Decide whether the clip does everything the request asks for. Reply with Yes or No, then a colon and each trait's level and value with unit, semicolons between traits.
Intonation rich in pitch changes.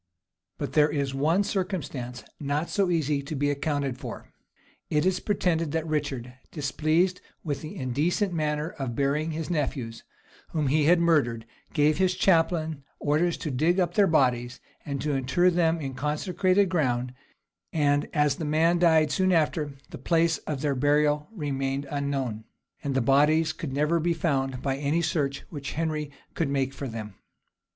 No: average, 3.2 semitones